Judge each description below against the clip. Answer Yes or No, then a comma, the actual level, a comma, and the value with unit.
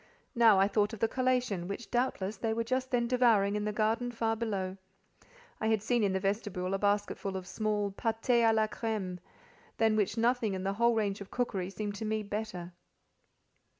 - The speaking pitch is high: Yes, high, 215 Hz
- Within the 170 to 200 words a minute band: Yes, average, 195 wpm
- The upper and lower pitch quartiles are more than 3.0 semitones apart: No, average, 2.7 semitones